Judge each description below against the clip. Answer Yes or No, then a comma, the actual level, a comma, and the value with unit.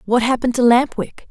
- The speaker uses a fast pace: Yes, fast, 230 wpm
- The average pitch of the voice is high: Yes, high, 240 Hz